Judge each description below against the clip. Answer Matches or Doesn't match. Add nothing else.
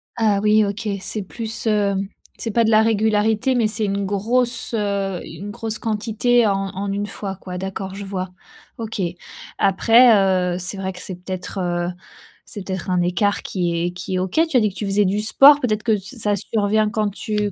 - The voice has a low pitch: Doesn't match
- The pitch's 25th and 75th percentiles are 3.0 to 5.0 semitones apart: Doesn't match